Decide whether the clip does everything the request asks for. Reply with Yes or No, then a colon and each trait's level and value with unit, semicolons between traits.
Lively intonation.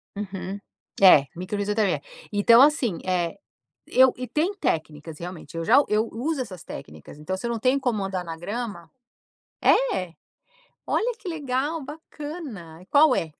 Yes: wide, 7.4 semitones